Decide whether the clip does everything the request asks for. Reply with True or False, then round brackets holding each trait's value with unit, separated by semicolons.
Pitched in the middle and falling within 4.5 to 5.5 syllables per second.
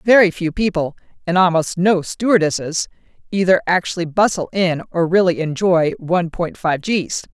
True (175 Hz; 5.0 syllables/s)